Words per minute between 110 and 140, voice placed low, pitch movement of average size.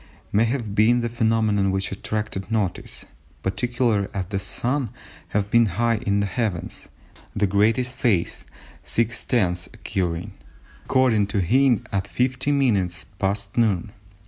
Yes: slow, 135 wpm; low, 105 Hz; average, 3.3 semitones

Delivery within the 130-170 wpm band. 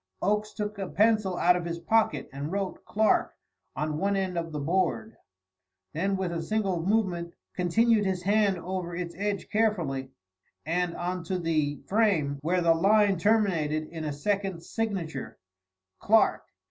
Yes: average, 155 wpm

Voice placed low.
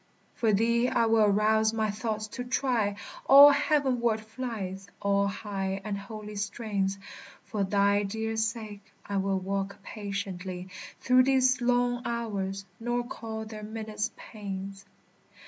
No: high, 215 Hz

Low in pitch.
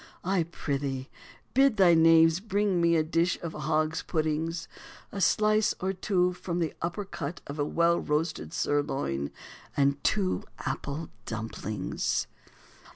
No: medium, 165 Hz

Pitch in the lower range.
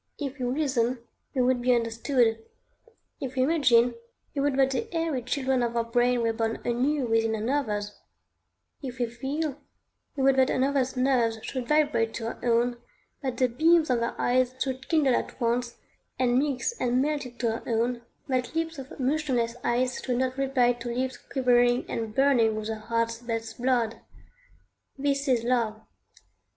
No: very high, 250 Hz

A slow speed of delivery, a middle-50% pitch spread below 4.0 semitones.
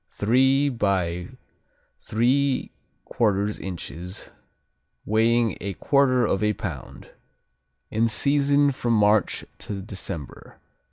No: slow, 90 wpm; average, 4.7 semitones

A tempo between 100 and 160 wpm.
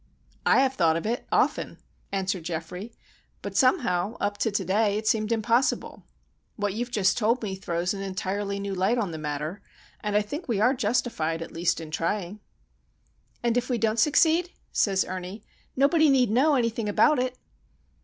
No: average, 175 wpm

